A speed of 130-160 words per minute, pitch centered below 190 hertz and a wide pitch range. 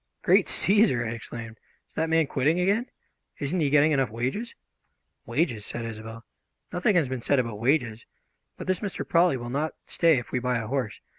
No: average, 190 wpm; low, 135 Hz; wide, 5.9 semitones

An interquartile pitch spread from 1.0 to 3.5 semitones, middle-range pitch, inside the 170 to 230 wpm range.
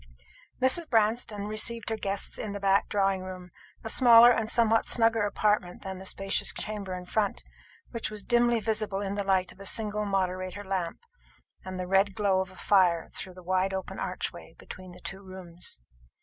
No: narrow, 2.5 semitones; high, 200 Hz; average, 185 wpm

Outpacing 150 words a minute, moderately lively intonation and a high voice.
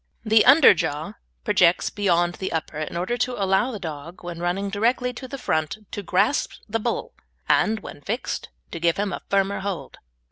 Yes: average, 180 wpm; average, 4.4 semitones; high, 195 Hz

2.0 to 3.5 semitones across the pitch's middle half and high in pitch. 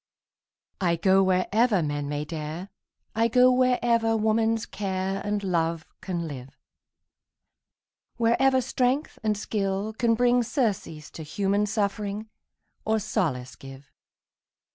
No: average, 5.2 semitones; high, 200 Hz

